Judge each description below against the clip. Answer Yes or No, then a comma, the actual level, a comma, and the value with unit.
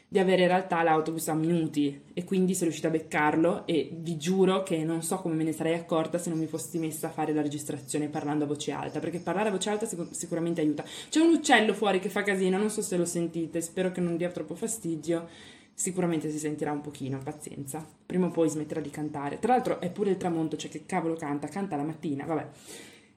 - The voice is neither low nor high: Yes, medium, 165 Hz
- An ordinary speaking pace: No, fast, 230 wpm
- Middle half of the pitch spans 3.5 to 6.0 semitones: No, average, 3.0 semitones